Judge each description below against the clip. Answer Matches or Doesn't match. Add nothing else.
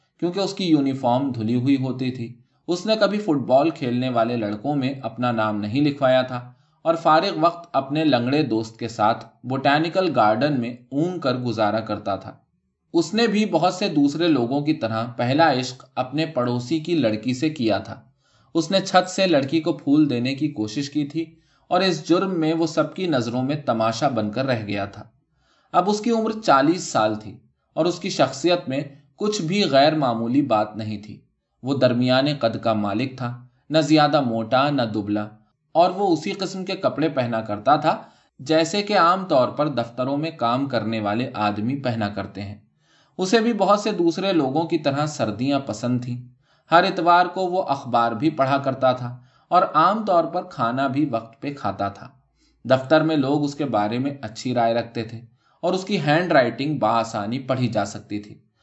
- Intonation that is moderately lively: Doesn't match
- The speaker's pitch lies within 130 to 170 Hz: Matches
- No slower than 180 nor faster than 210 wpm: Matches